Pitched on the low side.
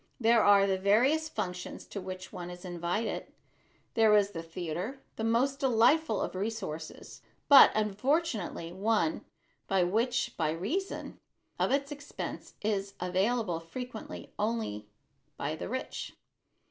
No: high, 210 Hz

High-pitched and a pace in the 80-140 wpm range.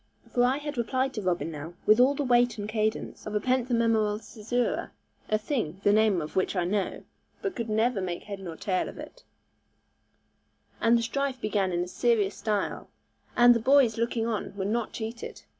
No: high, 220 Hz; average, 190 wpm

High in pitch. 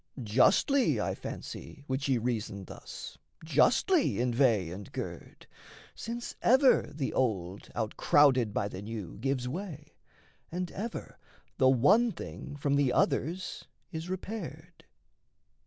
No: medium, 140 Hz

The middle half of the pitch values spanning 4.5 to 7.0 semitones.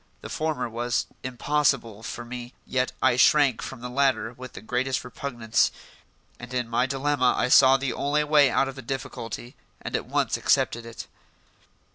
No: narrow, 2.4 semitones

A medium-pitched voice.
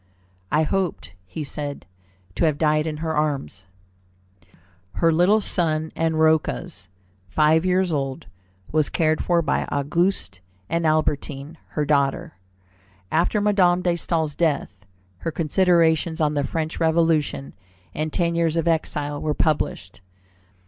Yes: medium, 155 Hz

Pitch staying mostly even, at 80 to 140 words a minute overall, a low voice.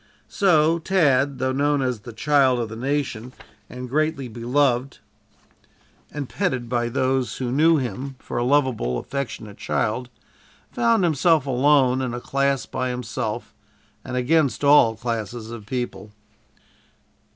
No: average, 3.1 semitones; slow, 135 wpm; low, 130 Hz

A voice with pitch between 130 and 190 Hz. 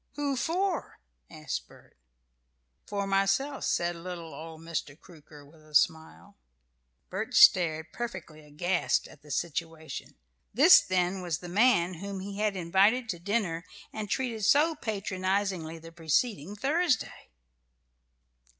Yes: medium, 185 Hz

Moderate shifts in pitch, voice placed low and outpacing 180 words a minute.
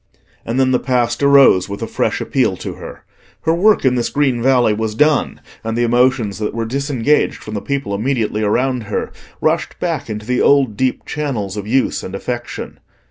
Yes: average, 4.1 semitones; low, 125 Hz; average, 190 wpm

